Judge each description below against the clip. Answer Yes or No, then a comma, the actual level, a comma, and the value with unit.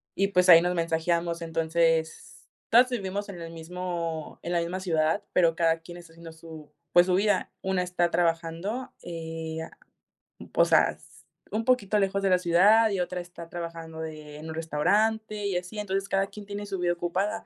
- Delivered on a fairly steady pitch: No, average, 3.1 semitones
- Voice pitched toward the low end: No, medium, 175 Hz